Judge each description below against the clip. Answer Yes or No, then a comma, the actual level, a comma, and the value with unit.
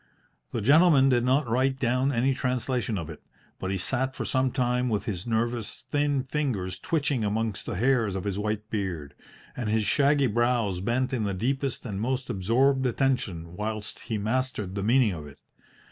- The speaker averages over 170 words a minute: Yes, average, 180 wpm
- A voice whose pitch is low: Yes, low, 120 Hz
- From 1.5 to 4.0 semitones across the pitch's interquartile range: No, average, 4.4 semitones